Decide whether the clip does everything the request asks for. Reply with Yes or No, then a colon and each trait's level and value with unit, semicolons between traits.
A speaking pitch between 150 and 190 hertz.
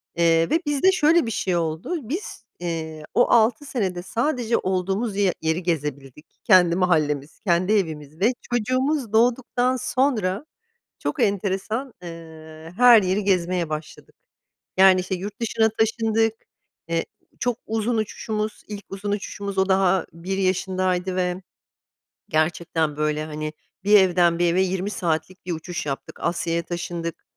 Yes: medium, 185 Hz